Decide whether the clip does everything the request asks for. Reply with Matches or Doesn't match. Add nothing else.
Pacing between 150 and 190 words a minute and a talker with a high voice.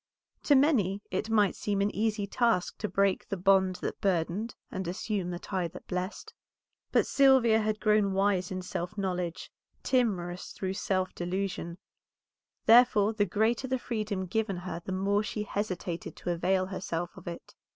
Matches